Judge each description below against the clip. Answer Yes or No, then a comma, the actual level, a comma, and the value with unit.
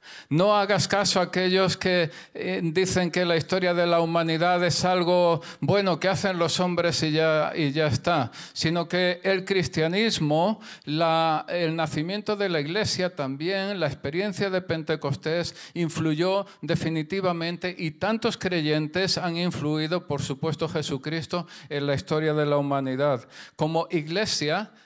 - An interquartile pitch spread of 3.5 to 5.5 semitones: No, average, 2.9 semitones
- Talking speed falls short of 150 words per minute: Yes, average, 140 wpm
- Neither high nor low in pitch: Yes, medium, 170 Hz